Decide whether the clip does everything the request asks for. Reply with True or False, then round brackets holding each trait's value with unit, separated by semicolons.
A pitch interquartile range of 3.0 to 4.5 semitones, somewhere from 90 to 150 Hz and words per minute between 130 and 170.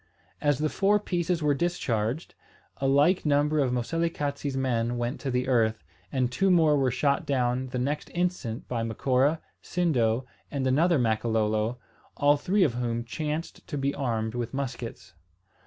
True (4.0 semitones; 135 Hz; 155 wpm)